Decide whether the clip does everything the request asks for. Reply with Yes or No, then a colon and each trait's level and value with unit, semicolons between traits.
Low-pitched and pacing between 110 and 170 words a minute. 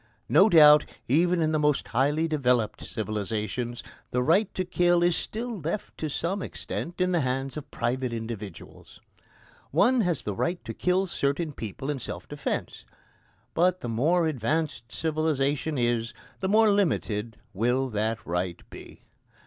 No: medium, 150 Hz; average, 150 wpm